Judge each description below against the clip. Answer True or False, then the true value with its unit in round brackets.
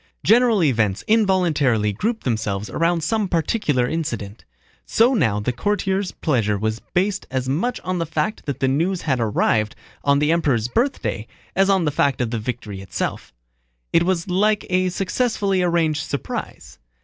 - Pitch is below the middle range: False (160 Hz)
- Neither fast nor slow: True (160 wpm)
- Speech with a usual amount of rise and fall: False (7.8 semitones)